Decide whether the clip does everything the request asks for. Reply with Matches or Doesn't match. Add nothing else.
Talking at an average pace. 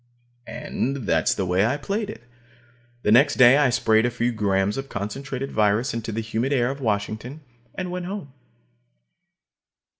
Matches